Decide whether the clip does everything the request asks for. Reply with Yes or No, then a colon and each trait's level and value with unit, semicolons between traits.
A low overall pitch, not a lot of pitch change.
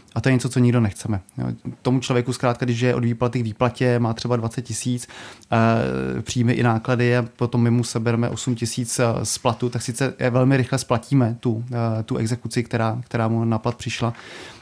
Yes: low, 120 Hz; narrow, 1.5 semitones